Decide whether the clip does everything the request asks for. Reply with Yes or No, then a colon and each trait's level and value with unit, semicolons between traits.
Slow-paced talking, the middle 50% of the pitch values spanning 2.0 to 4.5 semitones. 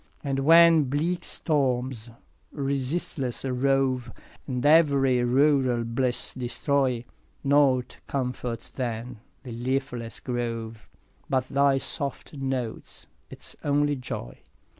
Yes: slow, 105 wpm; narrow, 2.4 semitones